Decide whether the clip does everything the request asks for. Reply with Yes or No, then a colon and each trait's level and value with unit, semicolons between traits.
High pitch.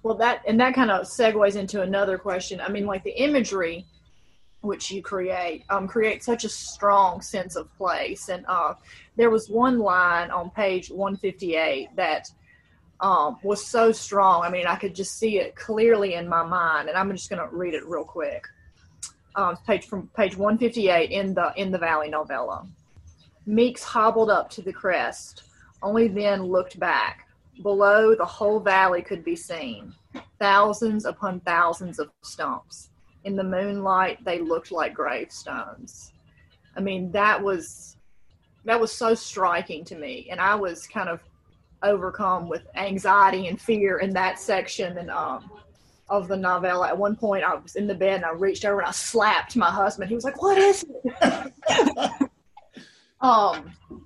Yes: high, 195 Hz